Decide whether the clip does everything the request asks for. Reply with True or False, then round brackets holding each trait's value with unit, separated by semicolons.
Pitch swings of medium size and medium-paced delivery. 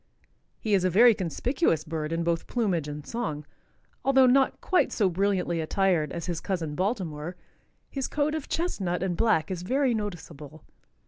False (6.2 semitones; 165 wpm)